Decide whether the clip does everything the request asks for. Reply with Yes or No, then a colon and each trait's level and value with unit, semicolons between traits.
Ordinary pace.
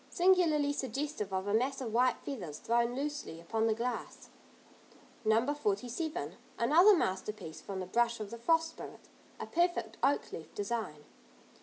Yes: average, 150 wpm